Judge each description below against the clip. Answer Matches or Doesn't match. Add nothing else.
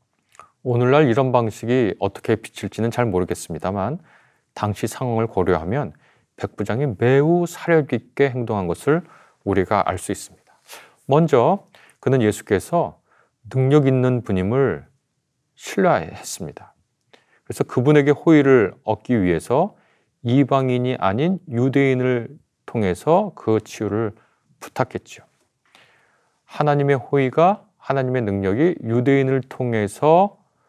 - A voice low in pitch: Matches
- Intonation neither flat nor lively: Matches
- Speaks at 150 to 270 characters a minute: Matches